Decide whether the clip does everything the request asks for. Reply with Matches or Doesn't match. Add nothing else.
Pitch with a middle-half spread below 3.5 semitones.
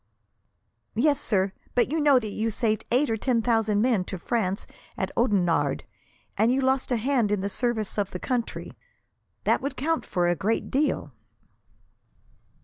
Doesn't match